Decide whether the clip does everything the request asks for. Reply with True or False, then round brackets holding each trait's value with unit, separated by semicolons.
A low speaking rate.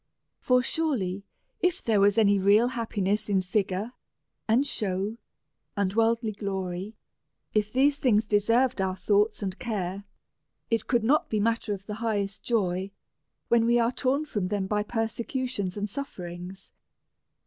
False (150 wpm)